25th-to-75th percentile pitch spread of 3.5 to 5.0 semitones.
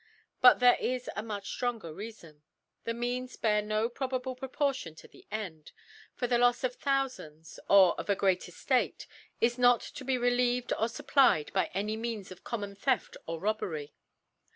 Yes: average, 4.0 semitones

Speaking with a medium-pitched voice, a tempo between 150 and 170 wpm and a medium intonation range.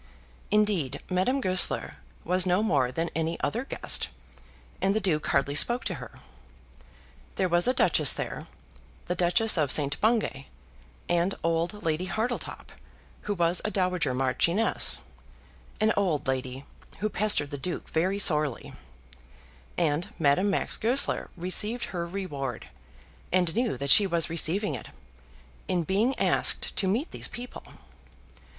No: medium, 180 Hz; average, 140 wpm; average, 4.8 semitones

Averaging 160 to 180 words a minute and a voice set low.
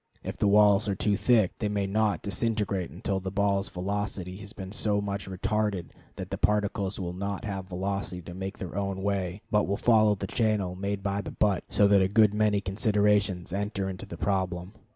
No: average, 200 wpm; low, 100 Hz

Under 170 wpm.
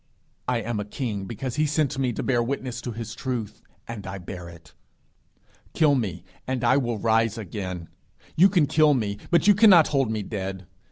No: average, 190 wpm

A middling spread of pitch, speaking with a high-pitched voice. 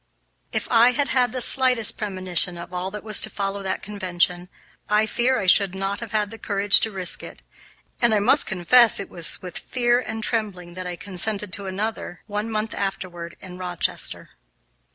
Yes: average, 3.3 semitones; high, 200 Hz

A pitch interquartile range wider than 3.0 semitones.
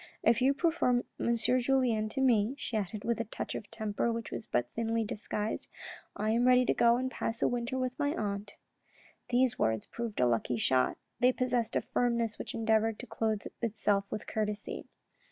No: average, 2.7 semitones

